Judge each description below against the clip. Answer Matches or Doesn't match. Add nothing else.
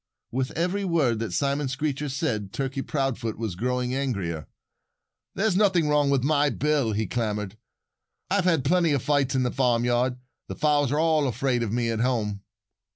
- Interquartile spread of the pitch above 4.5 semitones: Doesn't match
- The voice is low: Matches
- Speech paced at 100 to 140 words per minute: Doesn't match